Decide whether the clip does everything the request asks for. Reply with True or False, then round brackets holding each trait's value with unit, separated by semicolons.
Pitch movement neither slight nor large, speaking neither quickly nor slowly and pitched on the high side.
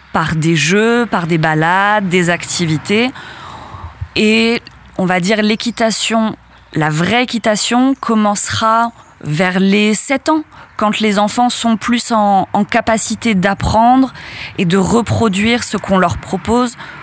False (3.5 semitones; 130 wpm; 215 Hz)